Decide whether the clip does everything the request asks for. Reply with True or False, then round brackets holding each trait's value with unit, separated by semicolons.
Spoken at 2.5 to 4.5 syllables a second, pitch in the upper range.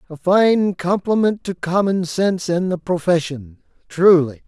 False (4.3 syllables/s; 175 Hz)